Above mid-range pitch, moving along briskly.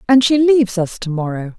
Yes: high, 215 Hz; fast, 225 wpm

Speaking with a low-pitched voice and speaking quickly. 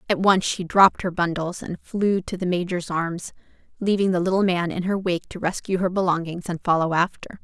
No: medium, 180 Hz; fast, 210 wpm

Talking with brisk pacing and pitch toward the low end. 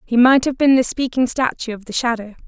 No: fast, 245 wpm; high, 245 Hz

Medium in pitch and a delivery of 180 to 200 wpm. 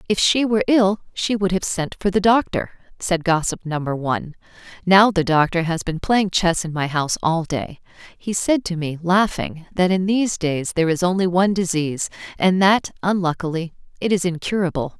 Yes: medium, 180 Hz; average, 190 wpm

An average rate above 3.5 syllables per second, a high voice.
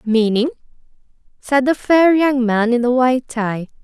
No: 3.3 syllables/s; very high, 250 Hz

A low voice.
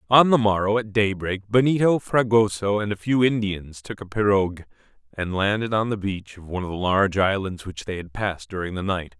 Yes: low, 100 Hz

